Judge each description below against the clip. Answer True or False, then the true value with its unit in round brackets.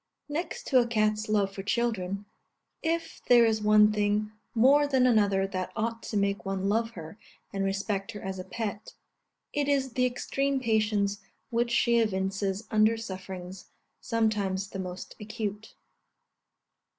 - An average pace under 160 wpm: True (150 wpm)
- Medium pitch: False (215 Hz)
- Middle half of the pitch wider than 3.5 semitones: False (3.0 semitones)